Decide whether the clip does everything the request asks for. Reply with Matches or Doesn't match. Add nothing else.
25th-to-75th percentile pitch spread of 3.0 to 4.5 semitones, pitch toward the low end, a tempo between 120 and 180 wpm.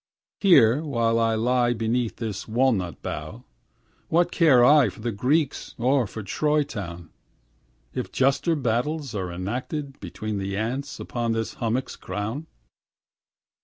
Matches